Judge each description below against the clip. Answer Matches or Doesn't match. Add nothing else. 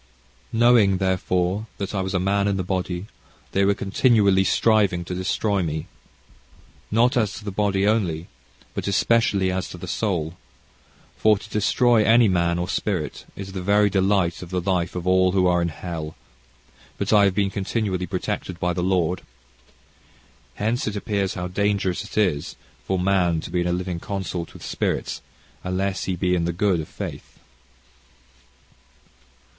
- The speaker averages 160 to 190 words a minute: Matches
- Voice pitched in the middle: Doesn't match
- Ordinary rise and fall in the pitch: Doesn't match